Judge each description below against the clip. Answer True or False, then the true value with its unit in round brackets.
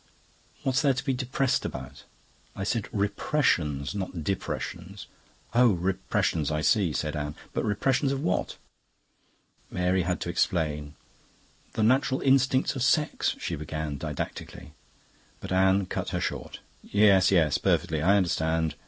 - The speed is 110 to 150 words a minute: True (135 wpm)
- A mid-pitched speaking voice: False (95 Hz)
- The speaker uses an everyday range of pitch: False (7.5 semitones)